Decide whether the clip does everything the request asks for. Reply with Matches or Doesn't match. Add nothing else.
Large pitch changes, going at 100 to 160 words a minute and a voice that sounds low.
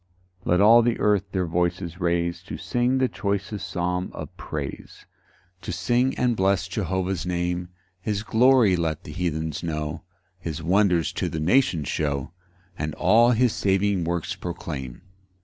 Doesn't match